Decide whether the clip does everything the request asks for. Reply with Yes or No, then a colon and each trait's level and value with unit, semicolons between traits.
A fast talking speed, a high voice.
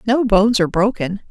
No: average, 185 wpm; high, 210 Hz